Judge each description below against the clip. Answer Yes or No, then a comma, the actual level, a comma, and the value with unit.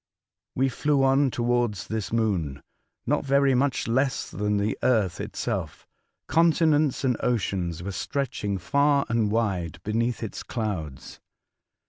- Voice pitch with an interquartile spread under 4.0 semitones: No, average, 5.0 semitones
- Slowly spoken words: Yes, slow, 130 wpm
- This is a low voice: Yes, low, 115 Hz